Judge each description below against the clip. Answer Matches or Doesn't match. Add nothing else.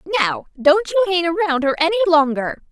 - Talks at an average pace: Matches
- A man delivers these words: Doesn't match